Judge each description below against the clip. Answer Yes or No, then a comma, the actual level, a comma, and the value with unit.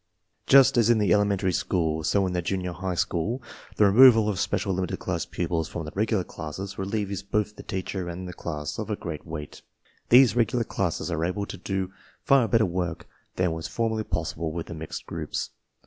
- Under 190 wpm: No, average, 200 wpm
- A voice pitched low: Yes, very low, 95 Hz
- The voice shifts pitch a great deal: No, average, 3.8 semitones